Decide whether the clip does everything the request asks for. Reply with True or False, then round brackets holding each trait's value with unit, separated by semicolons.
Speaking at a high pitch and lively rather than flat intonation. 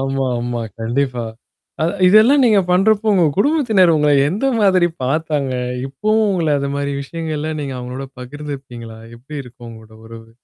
False (150 Hz; 6.8 semitones)